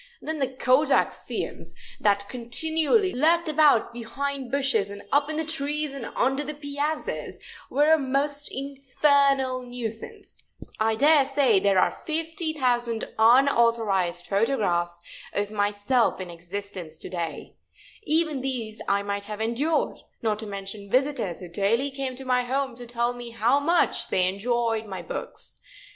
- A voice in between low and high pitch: No, very high, 250 Hz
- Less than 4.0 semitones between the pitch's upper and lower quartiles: No, average, 5.3 semitones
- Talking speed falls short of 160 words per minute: Yes, average, 150 wpm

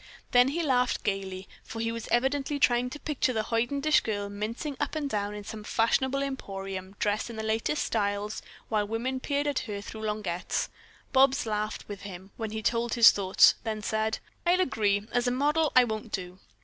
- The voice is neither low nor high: No, high, 225 Hz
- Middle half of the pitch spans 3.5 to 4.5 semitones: Yes, average, 4.2 semitones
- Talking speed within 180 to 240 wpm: Yes, average, 190 wpm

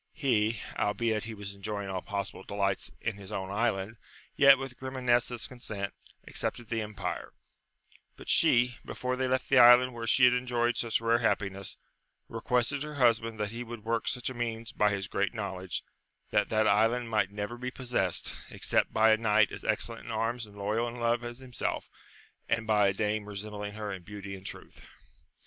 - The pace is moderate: Yes, average, 190 wpm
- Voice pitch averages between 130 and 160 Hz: No, low, 110 Hz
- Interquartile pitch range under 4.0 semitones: Yes, average, 2.8 semitones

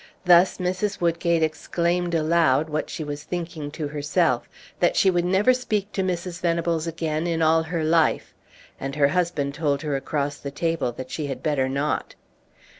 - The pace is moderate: Yes, average, 175 wpm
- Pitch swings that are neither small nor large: Yes, average, 3.0 semitones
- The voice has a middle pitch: Yes, medium, 165 Hz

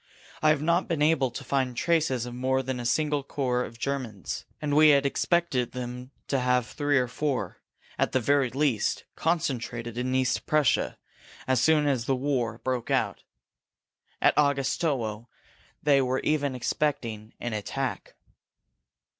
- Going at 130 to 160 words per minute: Yes, average, 155 wpm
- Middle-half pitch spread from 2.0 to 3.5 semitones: Yes, average, 2.9 semitones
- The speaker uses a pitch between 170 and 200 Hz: No, low, 130 Hz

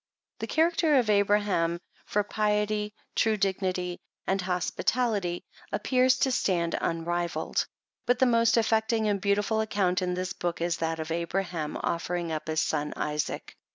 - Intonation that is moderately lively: Yes, average, 4.1 semitones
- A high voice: Yes, high, 195 Hz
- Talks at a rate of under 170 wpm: Yes, average, 150 wpm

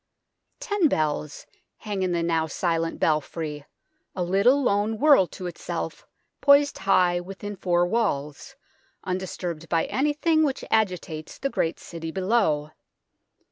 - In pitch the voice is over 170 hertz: Yes, medium, 185 Hz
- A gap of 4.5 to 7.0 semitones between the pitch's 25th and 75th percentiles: Yes, average, 5.3 semitones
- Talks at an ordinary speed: No, slow, 125 wpm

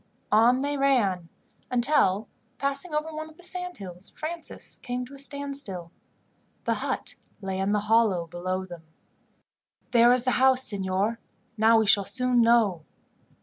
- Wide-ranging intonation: Yes, wide, 6.2 semitones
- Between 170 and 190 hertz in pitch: No, high, 235 Hz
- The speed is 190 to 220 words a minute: No, average, 150 wpm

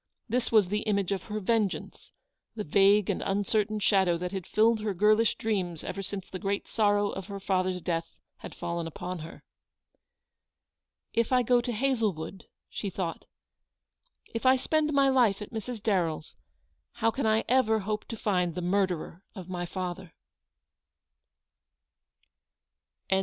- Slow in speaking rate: No, average, 150 wpm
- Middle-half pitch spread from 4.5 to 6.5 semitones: No, average, 3.3 semitones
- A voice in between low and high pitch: No, high, 200 Hz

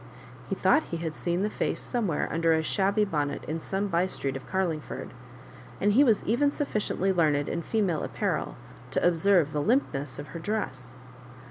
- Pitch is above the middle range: No, medium, 175 Hz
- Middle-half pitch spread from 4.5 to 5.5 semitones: Yes, average, 5.1 semitones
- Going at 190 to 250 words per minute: No, average, 175 wpm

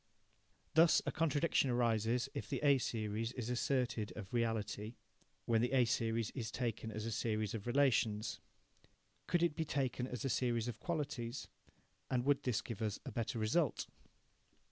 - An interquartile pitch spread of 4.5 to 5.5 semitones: No, average, 3.1 semitones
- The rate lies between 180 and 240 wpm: No, average, 165 wpm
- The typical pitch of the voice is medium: No, low, 120 Hz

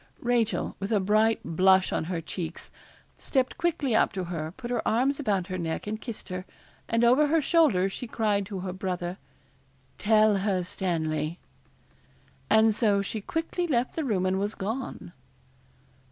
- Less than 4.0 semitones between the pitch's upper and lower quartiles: No, average, 4.4 semitones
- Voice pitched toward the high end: Yes, high, 205 Hz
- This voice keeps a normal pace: Yes, average, 165 wpm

